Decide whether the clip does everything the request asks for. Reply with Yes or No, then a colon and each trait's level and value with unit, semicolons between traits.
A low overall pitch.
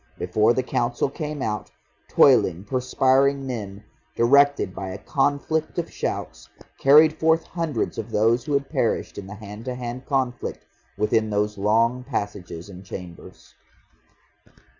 Yes: low, 120 Hz